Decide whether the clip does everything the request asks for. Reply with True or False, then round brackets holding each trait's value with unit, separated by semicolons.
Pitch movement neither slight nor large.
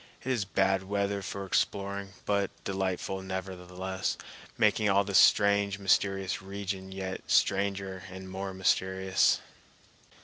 False (0.9 semitones)